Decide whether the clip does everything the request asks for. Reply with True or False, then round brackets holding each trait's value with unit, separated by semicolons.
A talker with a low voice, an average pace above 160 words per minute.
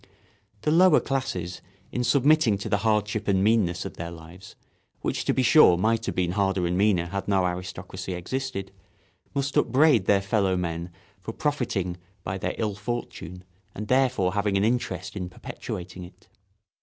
False (100 Hz; 155 wpm)